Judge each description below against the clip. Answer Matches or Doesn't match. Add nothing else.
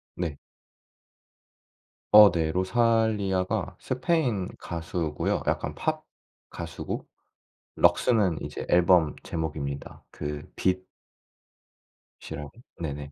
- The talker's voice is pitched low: Matches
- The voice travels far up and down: Doesn't match